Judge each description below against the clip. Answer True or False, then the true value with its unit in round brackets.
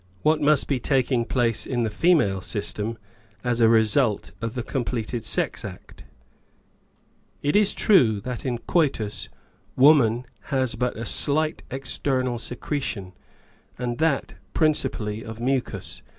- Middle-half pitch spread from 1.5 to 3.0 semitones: False (3.8 semitones)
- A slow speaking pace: True (130 wpm)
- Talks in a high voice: False (125 Hz)